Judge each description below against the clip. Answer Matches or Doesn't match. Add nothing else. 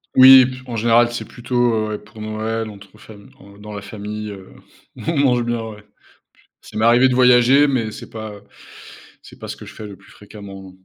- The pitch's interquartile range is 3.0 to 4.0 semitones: Doesn't match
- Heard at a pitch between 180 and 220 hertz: Doesn't match